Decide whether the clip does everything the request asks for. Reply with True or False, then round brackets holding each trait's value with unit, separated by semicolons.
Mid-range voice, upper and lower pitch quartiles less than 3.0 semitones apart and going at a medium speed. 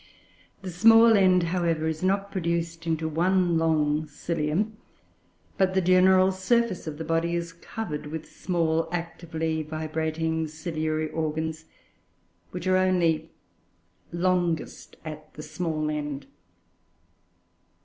False (165 Hz; 2.6 semitones; 115 wpm)